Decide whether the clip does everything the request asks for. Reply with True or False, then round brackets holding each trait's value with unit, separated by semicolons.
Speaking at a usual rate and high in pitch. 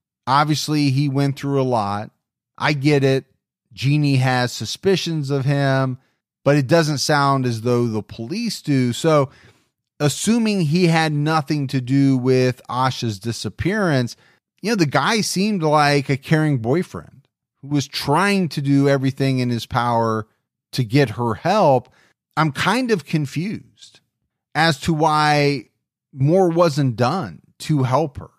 False (145 wpm; 140 Hz)